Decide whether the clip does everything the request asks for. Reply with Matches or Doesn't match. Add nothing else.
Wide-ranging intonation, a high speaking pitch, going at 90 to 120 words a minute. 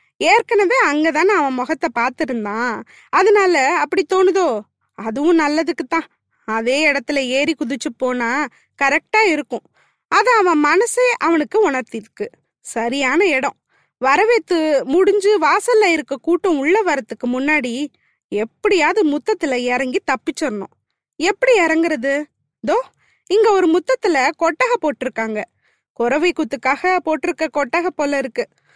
Matches